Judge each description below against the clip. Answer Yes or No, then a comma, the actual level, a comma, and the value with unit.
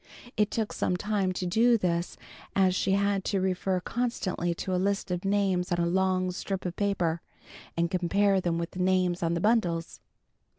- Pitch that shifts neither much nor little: No, narrow, 2.2 semitones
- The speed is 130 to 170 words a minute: No, average, 185 wpm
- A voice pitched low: No, medium, 185 Hz